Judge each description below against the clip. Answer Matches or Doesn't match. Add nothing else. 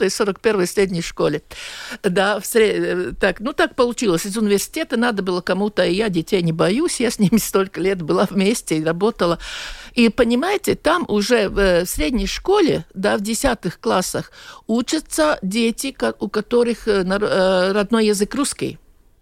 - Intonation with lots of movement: Doesn't match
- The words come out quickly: Doesn't match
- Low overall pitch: Doesn't match